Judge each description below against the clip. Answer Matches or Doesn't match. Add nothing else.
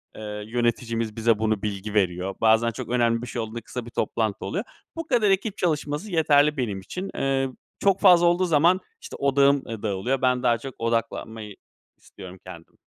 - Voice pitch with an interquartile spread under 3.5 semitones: Doesn't match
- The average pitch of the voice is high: Doesn't match